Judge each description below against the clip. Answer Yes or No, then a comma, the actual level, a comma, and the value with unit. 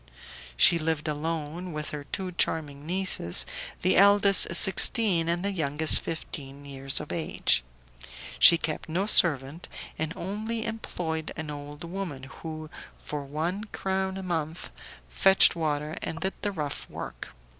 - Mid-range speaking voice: Yes, medium, 160 Hz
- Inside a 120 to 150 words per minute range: Yes, average, 140 wpm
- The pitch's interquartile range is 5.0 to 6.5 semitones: No, average, 4.2 semitones